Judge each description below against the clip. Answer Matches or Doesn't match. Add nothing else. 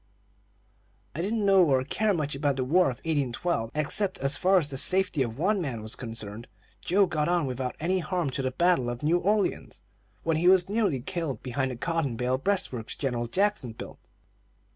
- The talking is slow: Doesn't match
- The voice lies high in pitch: Doesn't match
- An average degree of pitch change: Doesn't match